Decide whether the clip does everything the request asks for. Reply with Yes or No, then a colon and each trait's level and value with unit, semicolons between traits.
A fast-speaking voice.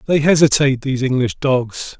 No: average, 150 wpm